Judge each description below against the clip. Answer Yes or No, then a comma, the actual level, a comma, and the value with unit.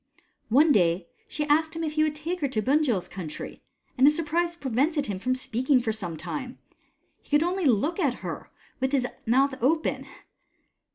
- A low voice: No, very high, 275 Hz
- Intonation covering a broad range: No, average, 4.7 semitones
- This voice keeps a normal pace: Yes, average, 180 wpm